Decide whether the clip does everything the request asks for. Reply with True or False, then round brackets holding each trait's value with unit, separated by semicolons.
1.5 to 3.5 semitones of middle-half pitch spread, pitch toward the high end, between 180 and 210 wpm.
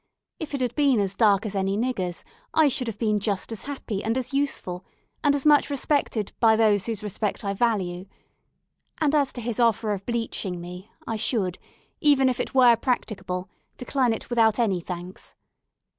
False (4.5 semitones; 225 Hz; 185 wpm)